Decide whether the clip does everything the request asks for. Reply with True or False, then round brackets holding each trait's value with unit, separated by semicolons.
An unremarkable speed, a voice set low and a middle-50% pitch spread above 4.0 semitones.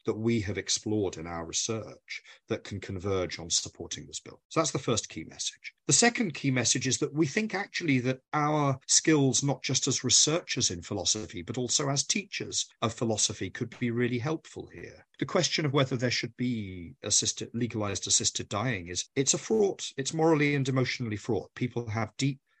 True (190 wpm; 125 Hz; 4.7 semitones)